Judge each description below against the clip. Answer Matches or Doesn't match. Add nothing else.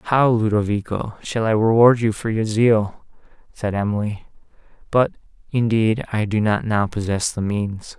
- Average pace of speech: Matches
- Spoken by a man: Matches